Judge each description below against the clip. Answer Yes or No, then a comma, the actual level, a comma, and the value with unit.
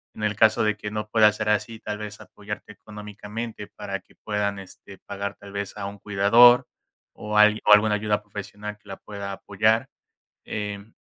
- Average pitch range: No, narrow, 0.9 semitones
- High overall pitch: No, low, 105 Hz